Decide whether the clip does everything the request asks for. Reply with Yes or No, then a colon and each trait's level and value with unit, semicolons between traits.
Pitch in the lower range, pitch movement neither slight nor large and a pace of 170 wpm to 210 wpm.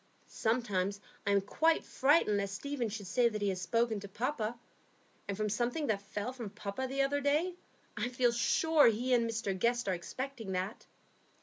No: high, 230 Hz; average, 4.2 semitones; average, 185 wpm